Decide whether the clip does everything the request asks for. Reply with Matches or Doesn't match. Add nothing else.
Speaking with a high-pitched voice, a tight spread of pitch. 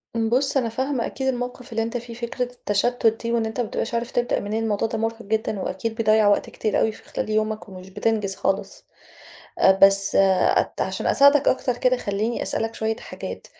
Matches